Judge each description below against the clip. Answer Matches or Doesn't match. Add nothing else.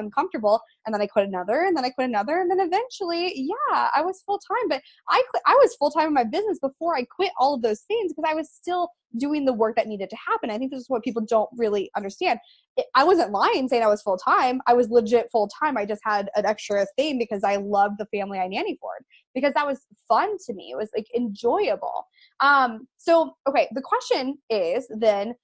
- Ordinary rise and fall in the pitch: Doesn't match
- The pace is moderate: Doesn't match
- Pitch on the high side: Matches